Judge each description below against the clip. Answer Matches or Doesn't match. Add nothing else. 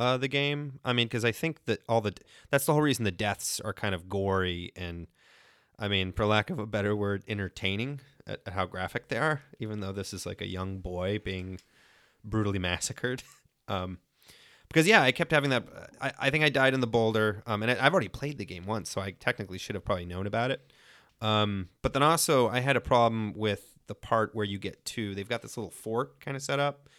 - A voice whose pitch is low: Matches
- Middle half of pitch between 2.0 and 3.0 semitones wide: Doesn't match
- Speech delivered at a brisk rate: Matches